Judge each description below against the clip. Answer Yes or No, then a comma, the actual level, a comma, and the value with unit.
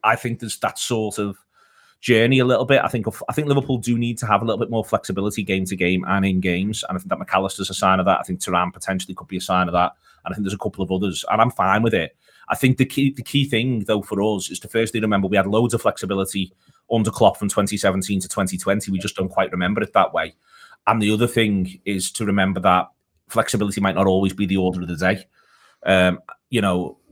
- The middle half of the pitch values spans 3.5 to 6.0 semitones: No, average, 3.0 semitones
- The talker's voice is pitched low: Yes, low, 100 Hz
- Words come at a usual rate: No, fast, 255 wpm